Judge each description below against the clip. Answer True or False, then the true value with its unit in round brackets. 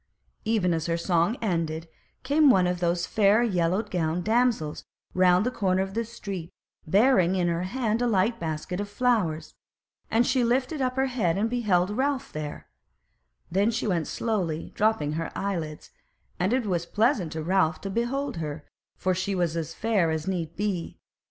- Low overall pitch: False (190 Hz)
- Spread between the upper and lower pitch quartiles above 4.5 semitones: True (5.3 semitones)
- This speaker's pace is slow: False (180 wpm)